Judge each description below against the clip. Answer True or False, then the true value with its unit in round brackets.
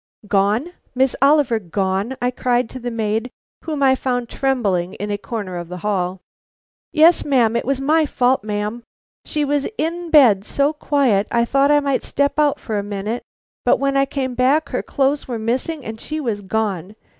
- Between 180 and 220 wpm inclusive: True (190 wpm)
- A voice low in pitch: False (245 Hz)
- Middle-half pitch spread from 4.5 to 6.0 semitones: True (5.1 semitones)